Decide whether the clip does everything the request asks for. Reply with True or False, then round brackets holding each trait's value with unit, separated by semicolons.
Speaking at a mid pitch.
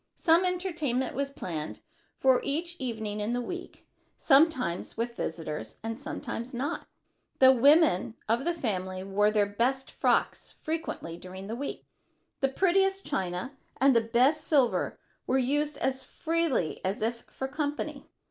False (260 Hz)